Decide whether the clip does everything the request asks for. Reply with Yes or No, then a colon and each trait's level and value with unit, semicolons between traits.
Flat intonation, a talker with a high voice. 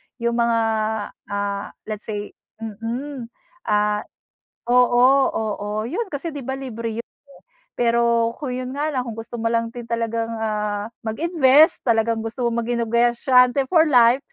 Yes: narrow, 2.1 semitones; high, 235 Hz